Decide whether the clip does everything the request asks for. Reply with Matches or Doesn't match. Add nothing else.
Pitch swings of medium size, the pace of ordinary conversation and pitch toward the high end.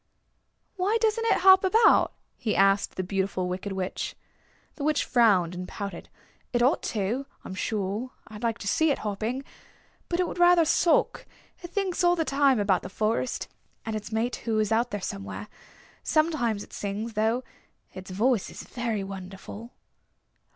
Doesn't match